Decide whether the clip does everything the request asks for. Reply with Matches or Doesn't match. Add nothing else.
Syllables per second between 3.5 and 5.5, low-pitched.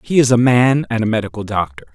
Doesn't match